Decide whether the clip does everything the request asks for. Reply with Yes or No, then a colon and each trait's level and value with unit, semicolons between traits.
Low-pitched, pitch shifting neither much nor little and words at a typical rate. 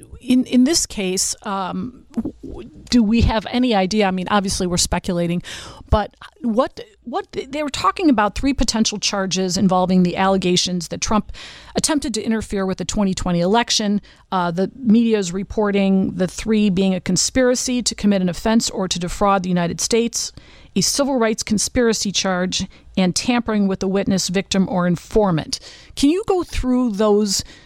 No: high, 205 Hz; average, 4.2 semitones; average, 165 wpm